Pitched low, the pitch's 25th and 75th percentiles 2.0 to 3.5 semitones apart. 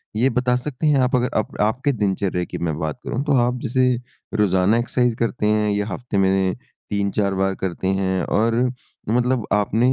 No: low, 110 Hz; average, 4.3 semitones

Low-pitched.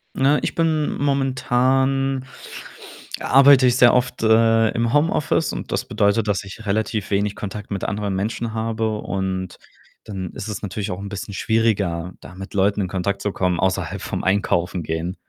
Yes: low, 105 Hz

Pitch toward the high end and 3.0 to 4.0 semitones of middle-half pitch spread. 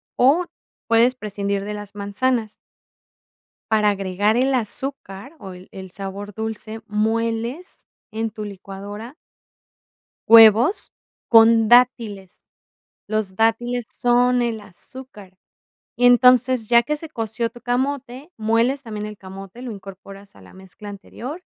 Yes: high, 225 Hz; average, 3.3 semitones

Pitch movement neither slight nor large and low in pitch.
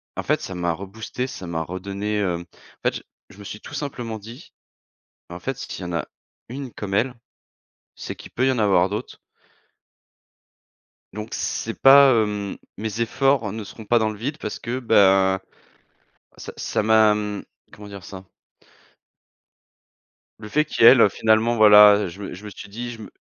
Yes: average, 3.0 semitones; low, 105 Hz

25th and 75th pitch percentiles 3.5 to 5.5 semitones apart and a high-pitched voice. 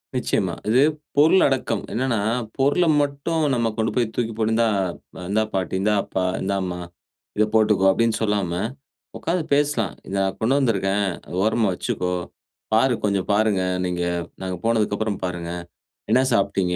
No: average, 4.0 semitones; low, 110 Hz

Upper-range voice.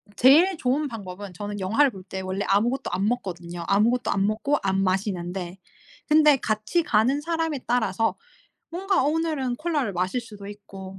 Yes: high, 215 Hz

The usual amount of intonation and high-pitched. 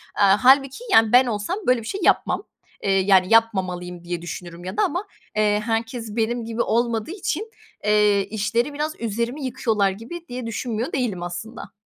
Yes: average, 3.7 semitones; high, 225 Hz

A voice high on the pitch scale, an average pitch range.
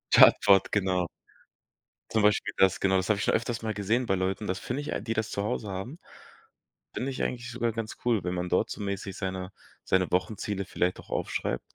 No: low, 100 Hz; average, 3.2 semitones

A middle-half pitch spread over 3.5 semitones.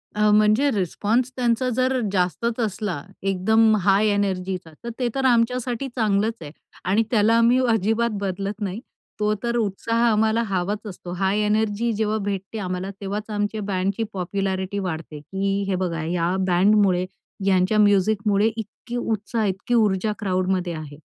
No: average, 2.8 semitones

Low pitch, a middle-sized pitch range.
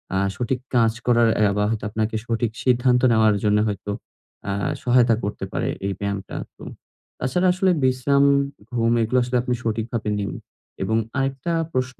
Yes: low, 115 Hz; average, 3.0 semitones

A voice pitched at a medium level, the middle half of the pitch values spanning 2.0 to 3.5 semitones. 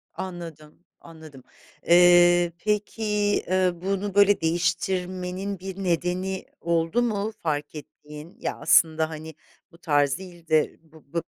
Yes: medium, 175 Hz; average, 2.8 semitones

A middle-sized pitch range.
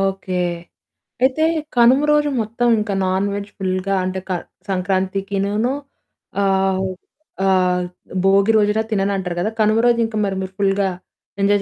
No: narrow, 2.2 semitones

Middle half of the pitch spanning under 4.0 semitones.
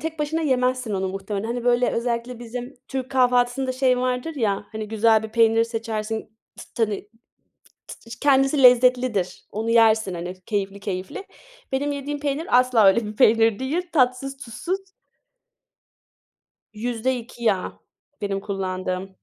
Yes: average, 3.3 semitones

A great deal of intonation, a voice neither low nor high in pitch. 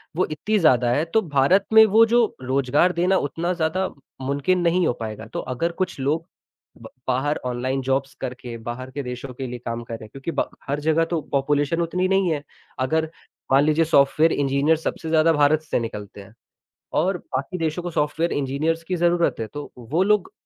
No: average, 4.5 semitones; medium, 150 Hz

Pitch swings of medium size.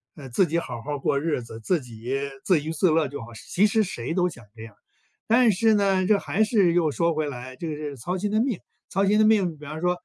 No: wide, 5.9 semitones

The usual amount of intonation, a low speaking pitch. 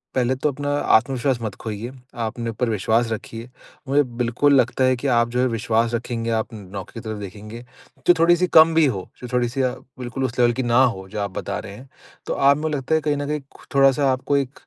Yes: average, 3.2 semitones; low, 125 Hz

